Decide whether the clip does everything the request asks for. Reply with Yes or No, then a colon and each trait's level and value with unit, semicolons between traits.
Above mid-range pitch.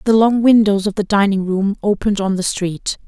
Yes: high, 205 Hz